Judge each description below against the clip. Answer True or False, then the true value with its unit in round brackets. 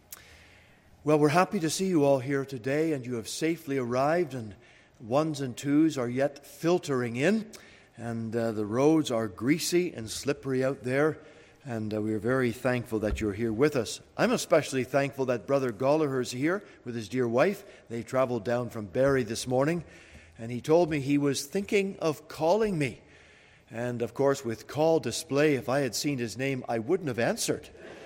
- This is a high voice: False (135 Hz)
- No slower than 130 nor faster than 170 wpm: False (185 wpm)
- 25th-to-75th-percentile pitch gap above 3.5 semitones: True (4.4 semitones)